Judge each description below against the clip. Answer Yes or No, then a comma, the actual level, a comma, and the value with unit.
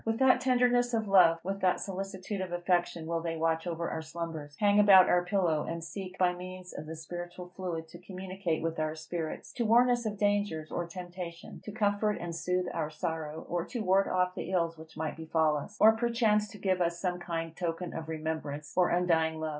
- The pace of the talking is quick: Yes, fast, 210 wpm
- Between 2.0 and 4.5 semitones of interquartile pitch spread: Yes, average, 3.2 semitones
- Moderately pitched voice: Yes, medium, 180 Hz